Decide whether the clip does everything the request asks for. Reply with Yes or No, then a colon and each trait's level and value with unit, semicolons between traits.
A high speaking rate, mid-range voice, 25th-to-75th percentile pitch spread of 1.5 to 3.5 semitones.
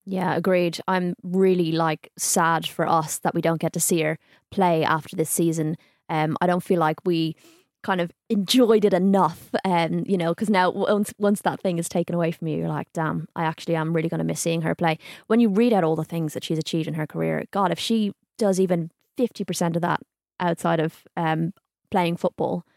Yes: fast, 220 wpm; medium, 170 Hz; average, 2.7 semitones